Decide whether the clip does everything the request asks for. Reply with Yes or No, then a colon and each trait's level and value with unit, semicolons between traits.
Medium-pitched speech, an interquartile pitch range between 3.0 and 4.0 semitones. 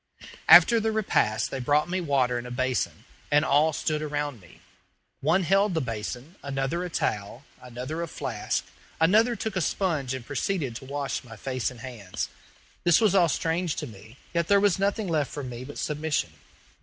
No: medium, 145 Hz; wide, 5.6 semitones